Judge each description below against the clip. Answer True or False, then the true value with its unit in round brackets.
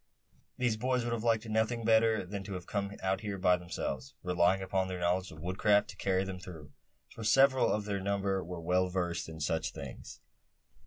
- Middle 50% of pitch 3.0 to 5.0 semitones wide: True (3.3 semitones)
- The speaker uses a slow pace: False (200 wpm)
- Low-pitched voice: True (95 Hz)